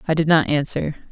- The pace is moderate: No, fast, 215 wpm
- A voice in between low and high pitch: Yes, medium, 155 Hz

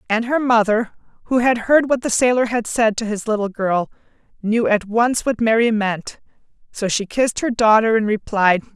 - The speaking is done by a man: No, female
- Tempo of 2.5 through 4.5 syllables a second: No, 4.9 syllables/s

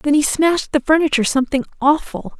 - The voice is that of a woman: Yes, female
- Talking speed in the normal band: Yes, average, 175 wpm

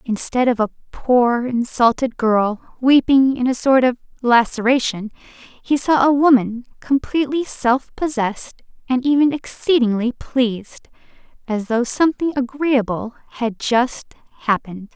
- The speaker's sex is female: Yes, female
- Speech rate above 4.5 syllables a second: No, 4.3 syllables/s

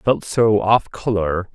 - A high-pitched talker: No, low, 100 Hz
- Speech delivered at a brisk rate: No, average, 155 wpm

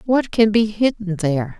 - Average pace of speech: Yes, average, 190 wpm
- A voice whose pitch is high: Yes, high, 200 Hz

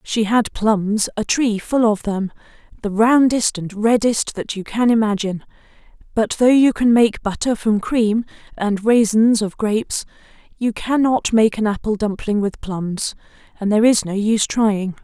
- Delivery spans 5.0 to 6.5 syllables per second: No, 4.5 syllables/s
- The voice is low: No, high, 220 Hz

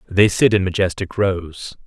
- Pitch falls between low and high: No, very low, 95 Hz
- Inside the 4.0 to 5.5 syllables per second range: Yes, 4.3 syllables/s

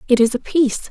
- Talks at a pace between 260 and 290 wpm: Yes, fast, 265 wpm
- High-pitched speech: Yes, very high, 255 Hz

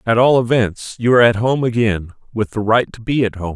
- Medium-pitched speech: No, low, 115 Hz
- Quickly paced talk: Yes, fast, 255 wpm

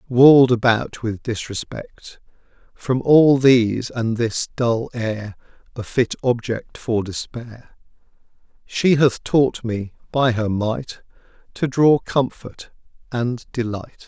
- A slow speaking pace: Yes, slow, 120 wpm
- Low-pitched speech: Yes, low, 120 Hz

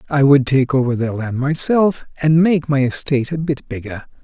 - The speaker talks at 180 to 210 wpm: Yes, average, 200 wpm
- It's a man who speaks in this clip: Yes, male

